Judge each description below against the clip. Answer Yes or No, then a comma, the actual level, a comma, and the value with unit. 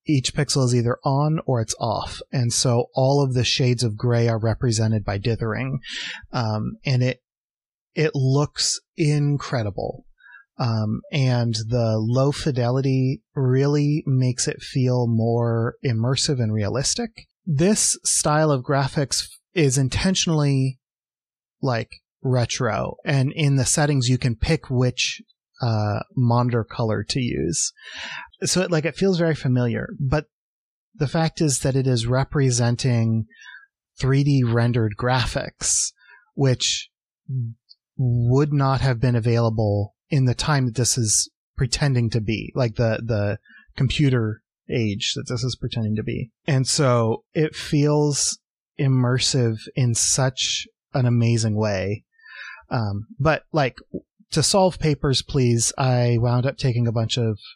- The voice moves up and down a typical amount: Yes, average, 3.4 semitones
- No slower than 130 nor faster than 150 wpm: Yes, slow, 135 wpm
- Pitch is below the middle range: Yes, low, 125 Hz